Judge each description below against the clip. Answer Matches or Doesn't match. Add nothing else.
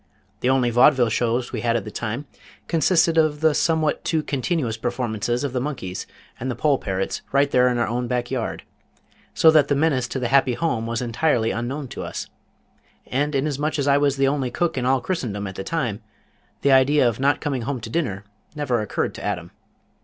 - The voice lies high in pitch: Doesn't match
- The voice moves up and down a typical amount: Matches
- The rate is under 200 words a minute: Doesn't match